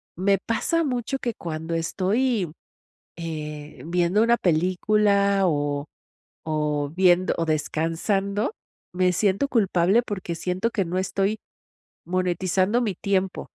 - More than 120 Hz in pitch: Yes, medium, 185 Hz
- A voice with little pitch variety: No, average, 3.8 semitones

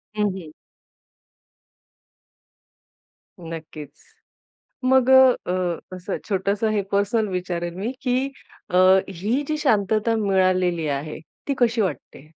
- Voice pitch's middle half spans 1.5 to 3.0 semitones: No, average, 4.4 semitones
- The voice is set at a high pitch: Yes, high, 195 Hz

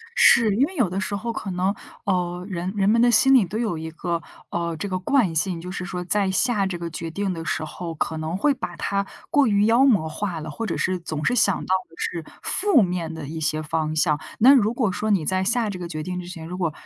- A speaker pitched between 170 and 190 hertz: Yes, medium, 185 Hz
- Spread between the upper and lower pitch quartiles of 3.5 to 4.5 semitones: Yes, average, 4.2 semitones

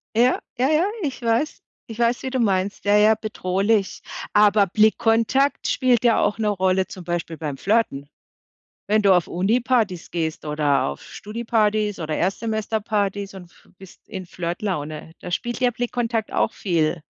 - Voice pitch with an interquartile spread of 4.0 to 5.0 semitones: Yes, average, 4.3 semitones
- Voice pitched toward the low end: No, high, 205 Hz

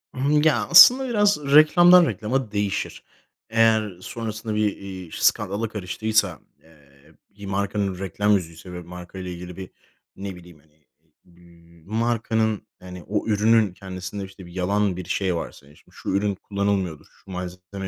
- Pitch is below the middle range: Yes, low, 100 Hz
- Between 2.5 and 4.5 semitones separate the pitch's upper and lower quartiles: Yes, average, 3.4 semitones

